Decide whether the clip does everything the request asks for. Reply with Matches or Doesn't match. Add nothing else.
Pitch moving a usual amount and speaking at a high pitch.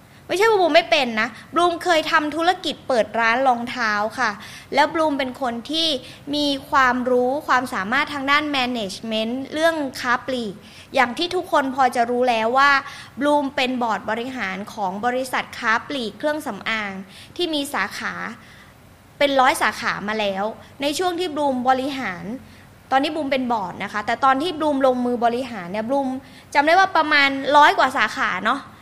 Matches